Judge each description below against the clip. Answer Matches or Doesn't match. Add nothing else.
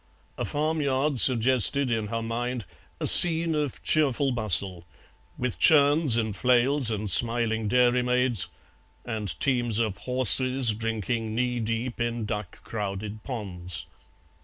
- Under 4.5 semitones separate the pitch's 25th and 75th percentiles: Matches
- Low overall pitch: Matches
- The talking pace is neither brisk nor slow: Doesn't match